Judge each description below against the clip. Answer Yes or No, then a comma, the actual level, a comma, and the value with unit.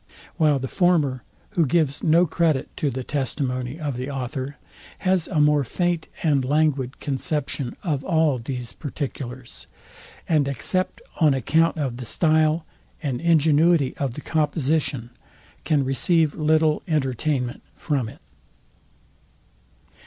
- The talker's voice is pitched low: No, medium, 145 Hz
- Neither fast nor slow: No, slow, 125 wpm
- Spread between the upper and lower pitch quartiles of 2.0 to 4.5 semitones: Yes, average, 3.2 semitones